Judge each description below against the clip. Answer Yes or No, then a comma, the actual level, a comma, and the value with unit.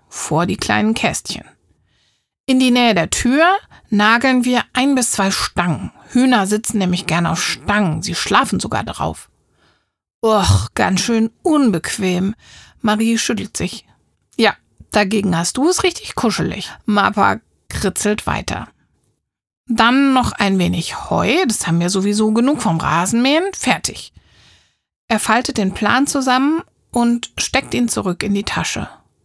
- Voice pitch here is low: No, high, 220 Hz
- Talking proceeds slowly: No, average, 135 wpm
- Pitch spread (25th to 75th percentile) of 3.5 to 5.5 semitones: Yes, average, 4.4 semitones